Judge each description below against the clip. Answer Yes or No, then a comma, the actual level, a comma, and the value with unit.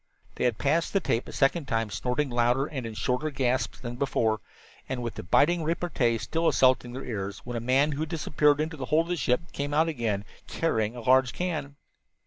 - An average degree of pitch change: Yes, average, 4.3 semitones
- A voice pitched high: No, low, 130 Hz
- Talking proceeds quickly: Yes, fast, 220 wpm